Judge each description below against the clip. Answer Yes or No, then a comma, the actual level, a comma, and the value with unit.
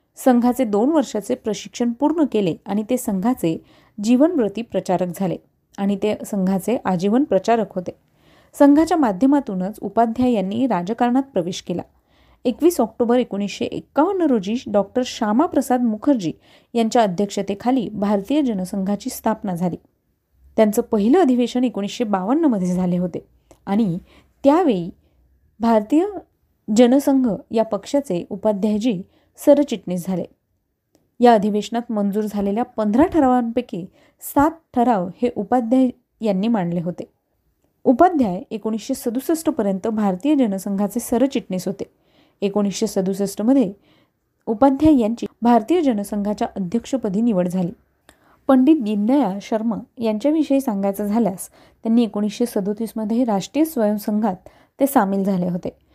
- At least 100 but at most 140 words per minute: Yes, average, 110 wpm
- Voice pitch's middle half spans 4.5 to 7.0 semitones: No, average, 4.1 semitones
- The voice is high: Yes, high, 225 Hz